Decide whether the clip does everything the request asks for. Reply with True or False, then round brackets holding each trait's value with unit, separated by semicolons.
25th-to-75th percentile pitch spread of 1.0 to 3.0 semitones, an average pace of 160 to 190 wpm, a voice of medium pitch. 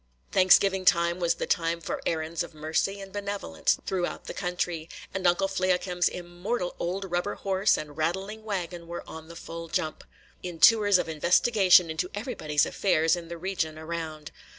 True (2.7 semitones; 165 wpm; 175 Hz)